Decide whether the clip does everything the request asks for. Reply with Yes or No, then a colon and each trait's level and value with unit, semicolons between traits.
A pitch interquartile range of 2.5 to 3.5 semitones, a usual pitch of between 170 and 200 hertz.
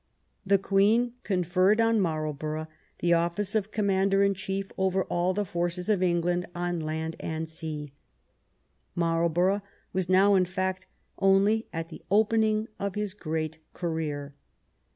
Yes: average, 3.1 semitones; medium, 185 Hz